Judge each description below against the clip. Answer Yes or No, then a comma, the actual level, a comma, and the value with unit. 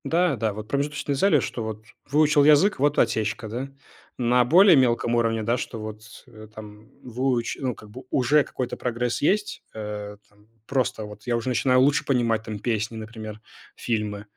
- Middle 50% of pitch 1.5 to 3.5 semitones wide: No, average, 3.9 semitones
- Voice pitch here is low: Yes, low, 120 Hz